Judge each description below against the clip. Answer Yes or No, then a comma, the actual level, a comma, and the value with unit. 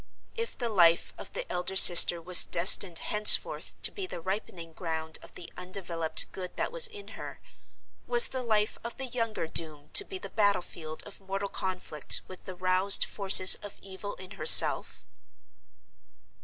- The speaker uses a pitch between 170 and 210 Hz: Yes, high, 190 Hz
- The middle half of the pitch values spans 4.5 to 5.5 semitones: No, average, 4.0 semitones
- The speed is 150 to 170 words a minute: Yes, average, 165 wpm